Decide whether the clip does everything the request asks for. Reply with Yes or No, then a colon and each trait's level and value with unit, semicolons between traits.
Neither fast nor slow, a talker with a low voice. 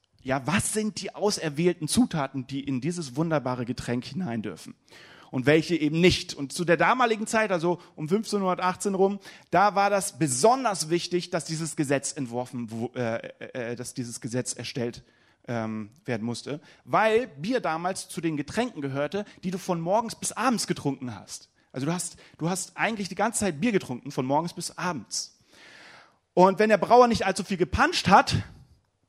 No: average, 165 wpm; medium, 165 Hz